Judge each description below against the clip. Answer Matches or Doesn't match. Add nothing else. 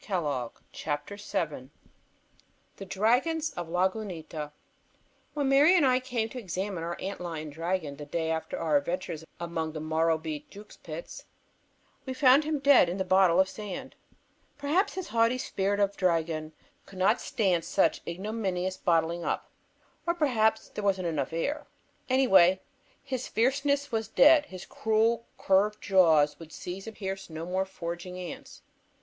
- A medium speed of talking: Matches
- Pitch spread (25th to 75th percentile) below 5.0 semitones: Doesn't match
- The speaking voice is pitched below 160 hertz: Doesn't match